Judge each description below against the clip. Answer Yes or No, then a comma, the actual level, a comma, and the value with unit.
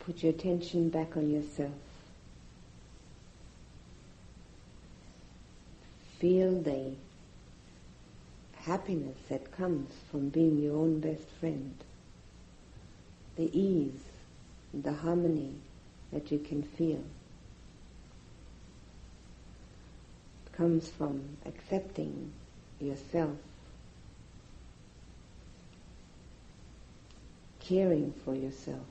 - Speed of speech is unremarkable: No, slow, 70 wpm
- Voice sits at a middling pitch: Yes, medium, 145 Hz